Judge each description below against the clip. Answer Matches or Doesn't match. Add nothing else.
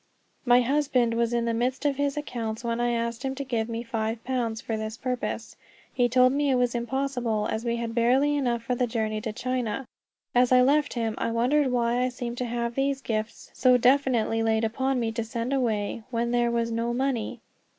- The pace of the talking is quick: Matches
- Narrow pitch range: Matches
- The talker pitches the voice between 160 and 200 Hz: Doesn't match